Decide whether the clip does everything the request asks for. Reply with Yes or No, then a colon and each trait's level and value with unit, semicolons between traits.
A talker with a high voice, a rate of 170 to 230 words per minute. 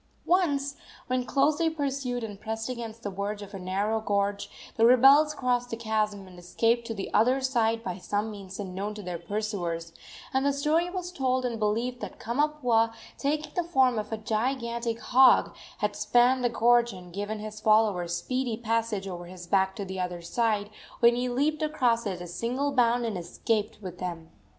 Yes: high, 225 Hz; average, 185 wpm